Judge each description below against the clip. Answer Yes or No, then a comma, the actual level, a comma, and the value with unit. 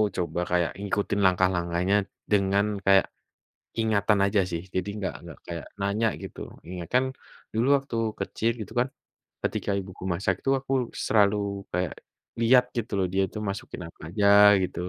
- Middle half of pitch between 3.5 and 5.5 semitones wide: No, average, 2.9 semitones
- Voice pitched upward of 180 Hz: No, low, 100 Hz